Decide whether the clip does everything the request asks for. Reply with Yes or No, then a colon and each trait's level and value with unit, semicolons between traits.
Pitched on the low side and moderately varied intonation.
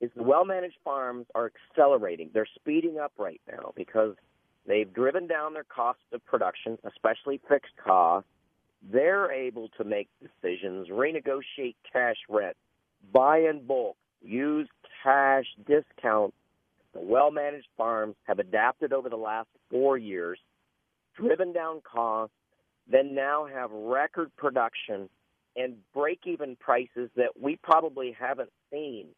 Yes: low, 130 Hz; average, 4.6 semitones